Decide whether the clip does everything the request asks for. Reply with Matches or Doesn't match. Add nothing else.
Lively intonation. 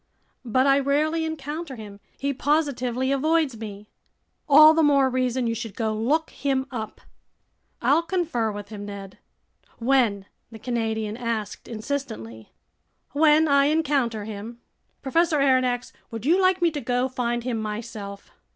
Doesn't match